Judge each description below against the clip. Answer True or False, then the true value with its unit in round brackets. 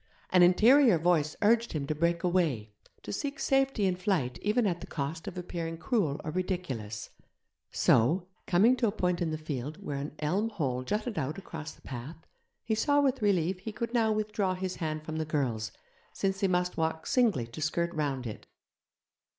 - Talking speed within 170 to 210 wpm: True (190 wpm)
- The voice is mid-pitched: True (175 Hz)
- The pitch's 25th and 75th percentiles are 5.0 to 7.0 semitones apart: True (5.4 semitones)